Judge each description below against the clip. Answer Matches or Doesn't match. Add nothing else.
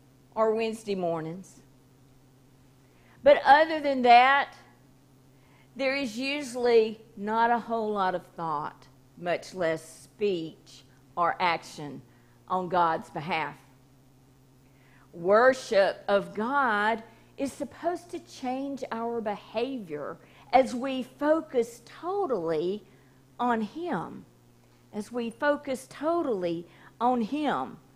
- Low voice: Doesn't match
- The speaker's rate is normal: Doesn't match